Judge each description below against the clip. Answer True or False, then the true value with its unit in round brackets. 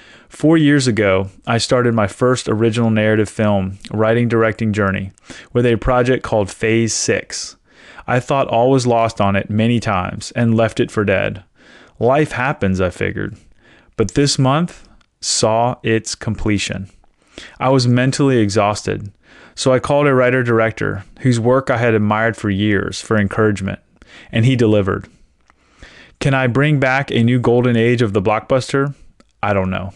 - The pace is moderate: True (160 wpm)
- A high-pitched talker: False (115 Hz)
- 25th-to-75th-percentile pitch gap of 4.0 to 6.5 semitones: False (3.3 semitones)